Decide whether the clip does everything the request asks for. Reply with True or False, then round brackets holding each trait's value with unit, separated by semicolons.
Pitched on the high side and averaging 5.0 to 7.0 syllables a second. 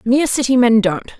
True (235 Hz; 5.8 syllables/s)